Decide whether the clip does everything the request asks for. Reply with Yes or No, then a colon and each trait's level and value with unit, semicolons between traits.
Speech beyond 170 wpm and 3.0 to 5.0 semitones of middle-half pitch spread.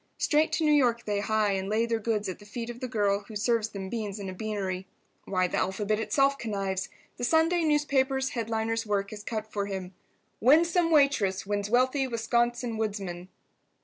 Yes: average, 185 wpm; average, 3.9 semitones